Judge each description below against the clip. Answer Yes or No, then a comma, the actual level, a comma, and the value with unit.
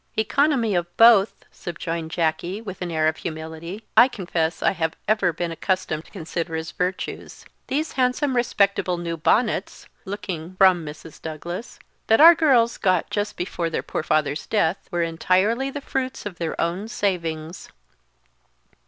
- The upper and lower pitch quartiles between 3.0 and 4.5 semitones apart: No, average, 5.0 semitones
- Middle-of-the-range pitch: Yes, medium, 180 Hz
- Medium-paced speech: Yes, average, 155 wpm